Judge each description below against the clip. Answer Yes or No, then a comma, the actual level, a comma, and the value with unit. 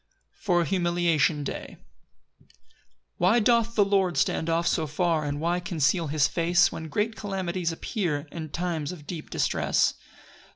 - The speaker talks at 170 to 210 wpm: No, average, 155 wpm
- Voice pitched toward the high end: No, medium, 170 Hz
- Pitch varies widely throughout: No, average, 2.8 semitones